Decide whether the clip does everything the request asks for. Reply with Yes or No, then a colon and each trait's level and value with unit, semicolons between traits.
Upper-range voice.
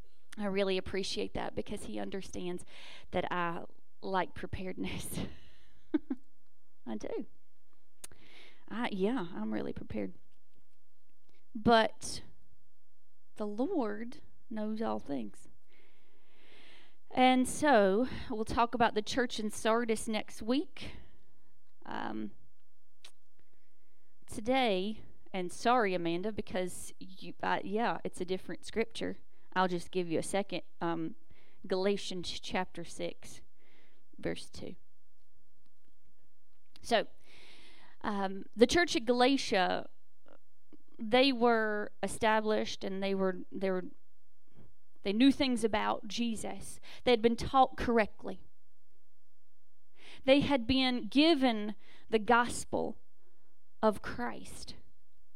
Yes: high, 215 Hz